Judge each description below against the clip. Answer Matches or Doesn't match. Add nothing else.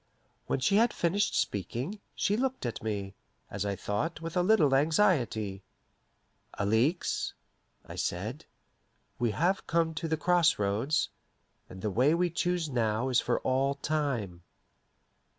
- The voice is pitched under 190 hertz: Matches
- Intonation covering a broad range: Matches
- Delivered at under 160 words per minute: Matches